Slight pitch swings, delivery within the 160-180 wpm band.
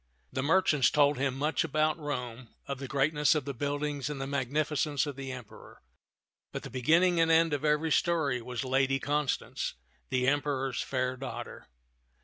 Yes: narrow, 2.3 semitones; average, 165 wpm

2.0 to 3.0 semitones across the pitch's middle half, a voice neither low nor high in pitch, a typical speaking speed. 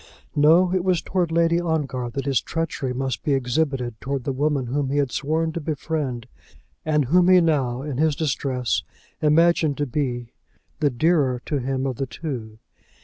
No: average, 3.7 semitones; medium, 145 Hz; average, 175 wpm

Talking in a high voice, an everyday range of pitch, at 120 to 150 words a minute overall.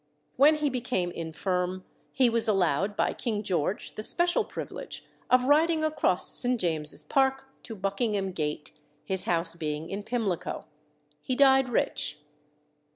No: high, 205 Hz; wide, 6.5 semitones; average, 140 wpm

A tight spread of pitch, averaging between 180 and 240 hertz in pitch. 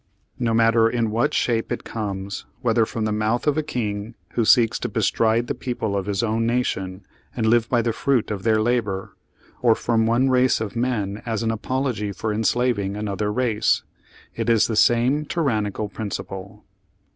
No: narrow, 2.3 semitones; low, 115 Hz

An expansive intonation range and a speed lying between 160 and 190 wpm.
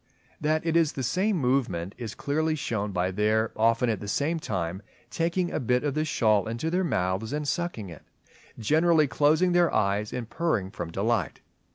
Yes: wide, 7.3 semitones; average, 185 wpm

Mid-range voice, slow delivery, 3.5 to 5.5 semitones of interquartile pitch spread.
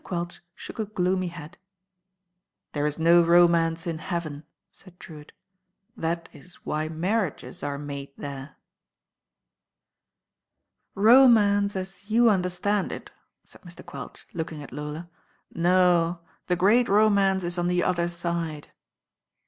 No: medium, 175 Hz; slow, 125 wpm; average, 2.9 semitones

